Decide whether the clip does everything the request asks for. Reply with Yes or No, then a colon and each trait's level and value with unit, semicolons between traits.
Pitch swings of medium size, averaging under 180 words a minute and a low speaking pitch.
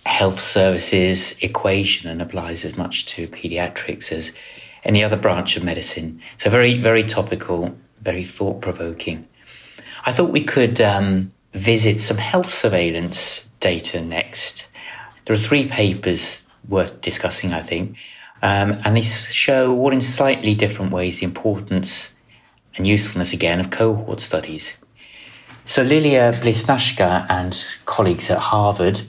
Yes: average, 3.8 semitones; slow, 135 wpm; low, 100 Hz